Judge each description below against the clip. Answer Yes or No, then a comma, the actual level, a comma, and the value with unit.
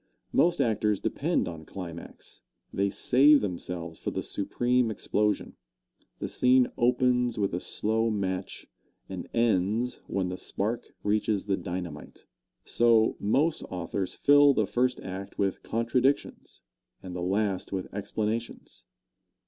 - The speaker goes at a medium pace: No, slow, 125 wpm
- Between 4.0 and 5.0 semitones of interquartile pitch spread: Yes, average, 4.5 semitones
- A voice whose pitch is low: Yes, low, 105 Hz